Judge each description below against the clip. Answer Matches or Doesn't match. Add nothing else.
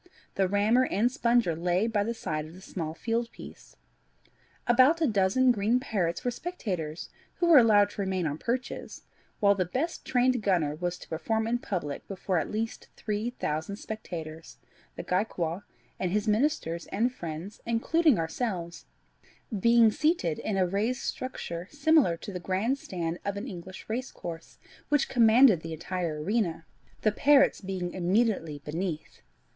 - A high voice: Matches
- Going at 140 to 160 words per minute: Matches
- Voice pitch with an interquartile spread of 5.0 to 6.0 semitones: Matches